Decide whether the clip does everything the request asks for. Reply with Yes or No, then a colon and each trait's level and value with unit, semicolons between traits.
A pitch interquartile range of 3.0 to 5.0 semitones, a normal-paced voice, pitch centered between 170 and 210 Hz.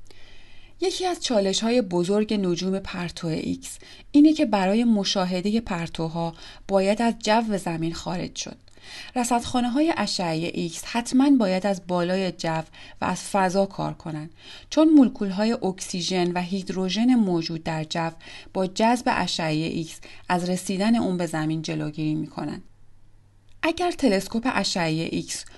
No: wide, 5.4 semitones; average, 135 wpm; medium, 185 Hz